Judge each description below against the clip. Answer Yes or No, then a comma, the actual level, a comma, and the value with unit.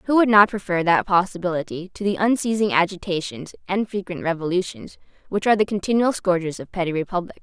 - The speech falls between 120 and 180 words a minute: Yes, average, 170 wpm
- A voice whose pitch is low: No, medium, 185 Hz